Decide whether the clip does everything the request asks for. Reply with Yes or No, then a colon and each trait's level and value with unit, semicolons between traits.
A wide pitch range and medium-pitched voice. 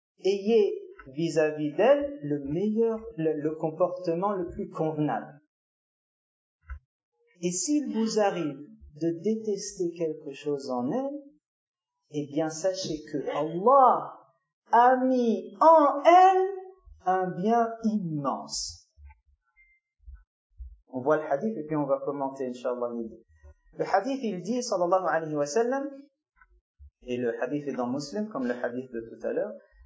Yes: wide, 9.0 semitones; medium, 165 Hz